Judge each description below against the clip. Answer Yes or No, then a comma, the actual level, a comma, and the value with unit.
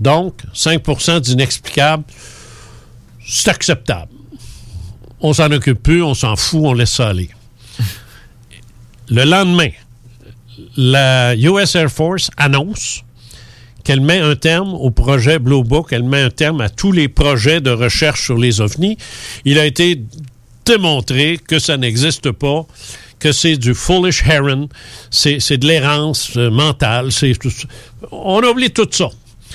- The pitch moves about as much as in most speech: Yes, average, 4.6 semitones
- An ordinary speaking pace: No, slow, 140 wpm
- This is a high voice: No, low, 135 Hz